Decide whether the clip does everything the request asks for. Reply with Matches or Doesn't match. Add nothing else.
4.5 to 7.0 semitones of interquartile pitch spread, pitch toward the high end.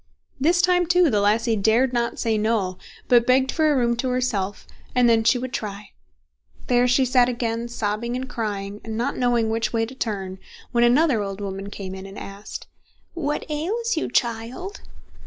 Doesn't match